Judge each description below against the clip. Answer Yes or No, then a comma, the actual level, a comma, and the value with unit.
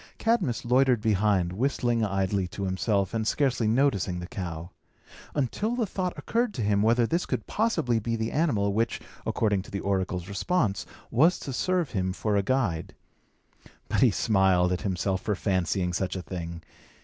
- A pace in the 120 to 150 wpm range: No, average, 170 wpm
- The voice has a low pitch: Yes, low, 105 Hz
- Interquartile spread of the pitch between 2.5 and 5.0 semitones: No, wide, 5.5 semitones